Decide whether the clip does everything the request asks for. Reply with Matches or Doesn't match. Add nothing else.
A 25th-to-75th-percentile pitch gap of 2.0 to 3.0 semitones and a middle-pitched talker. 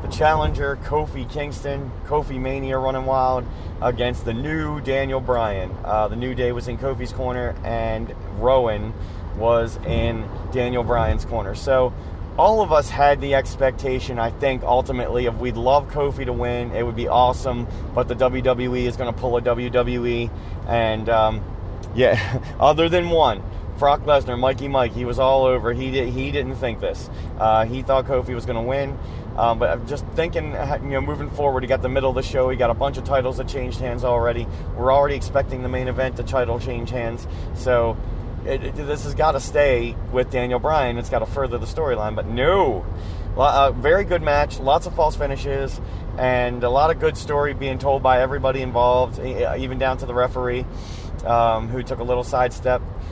Doesn't match